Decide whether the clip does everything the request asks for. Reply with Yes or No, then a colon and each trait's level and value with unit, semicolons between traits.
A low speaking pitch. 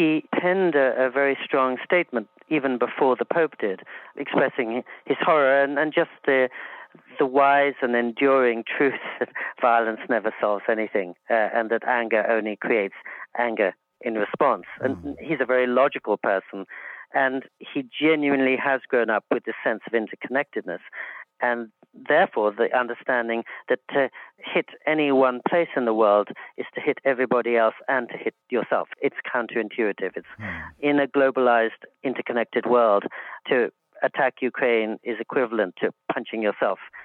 Yes: low, 125 Hz